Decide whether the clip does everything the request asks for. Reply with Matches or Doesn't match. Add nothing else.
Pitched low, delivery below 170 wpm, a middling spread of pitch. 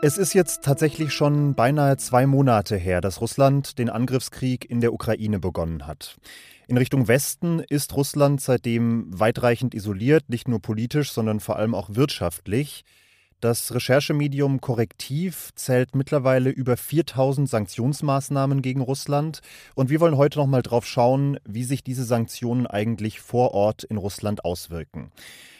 Matches